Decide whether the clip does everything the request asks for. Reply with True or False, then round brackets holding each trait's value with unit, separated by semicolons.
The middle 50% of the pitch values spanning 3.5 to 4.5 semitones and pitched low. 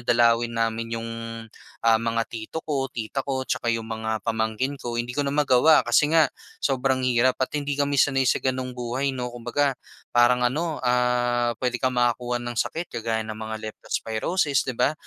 False (2.6 semitones; 125 Hz)